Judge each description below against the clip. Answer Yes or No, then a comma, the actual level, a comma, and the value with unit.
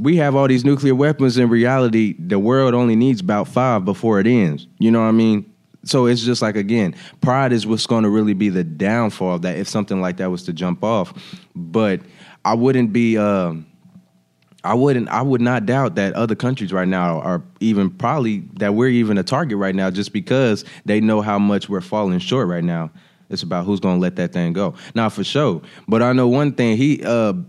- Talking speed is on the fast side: Yes, fast, 225 wpm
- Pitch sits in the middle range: No, low, 110 Hz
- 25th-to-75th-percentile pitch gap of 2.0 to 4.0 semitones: No, average, 4.5 semitones